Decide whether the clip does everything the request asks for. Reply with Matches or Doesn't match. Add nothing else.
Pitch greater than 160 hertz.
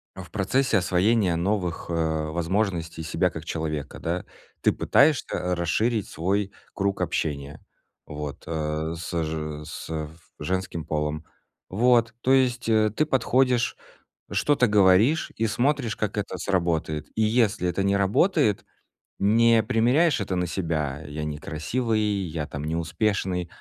Doesn't match